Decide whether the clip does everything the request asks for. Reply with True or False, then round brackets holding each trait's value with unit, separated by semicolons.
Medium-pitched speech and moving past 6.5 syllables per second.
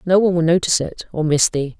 True (165 Hz; 6.8 syllables/s)